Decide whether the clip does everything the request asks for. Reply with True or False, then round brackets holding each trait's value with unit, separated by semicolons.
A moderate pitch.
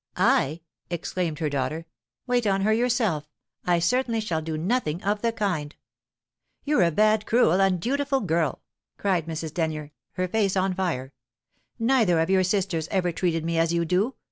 True (180 Hz)